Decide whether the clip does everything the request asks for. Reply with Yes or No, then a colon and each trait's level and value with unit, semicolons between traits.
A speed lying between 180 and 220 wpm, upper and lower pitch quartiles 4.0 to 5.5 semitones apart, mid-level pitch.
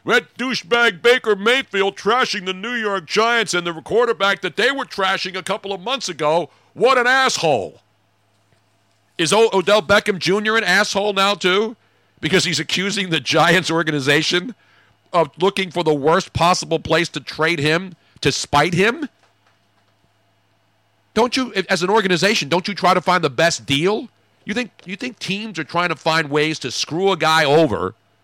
No: average, 170 wpm; average, 5.1 semitones; medium, 180 Hz